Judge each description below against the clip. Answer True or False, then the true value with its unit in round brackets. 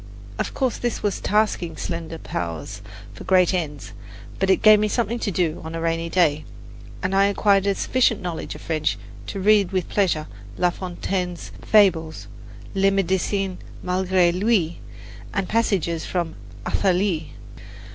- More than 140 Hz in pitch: True (185 Hz)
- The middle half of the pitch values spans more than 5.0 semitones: False (3.2 semitones)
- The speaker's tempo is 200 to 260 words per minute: False (145 wpm)